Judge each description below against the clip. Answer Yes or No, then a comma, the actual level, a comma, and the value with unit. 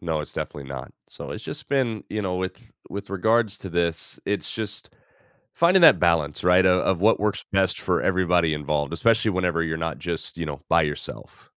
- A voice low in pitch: Yes, very low, 90 Hz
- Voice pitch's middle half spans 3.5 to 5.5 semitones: Yes, average, 4.0 semitones